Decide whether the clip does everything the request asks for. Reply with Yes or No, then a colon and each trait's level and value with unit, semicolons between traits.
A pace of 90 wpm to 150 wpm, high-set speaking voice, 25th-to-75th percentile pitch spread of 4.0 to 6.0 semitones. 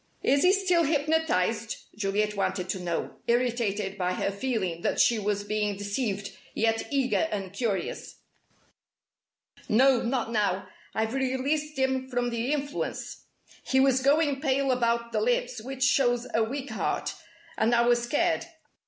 Yes: average, 145 wpm; high, 240 Hz; average, 4.3 semitones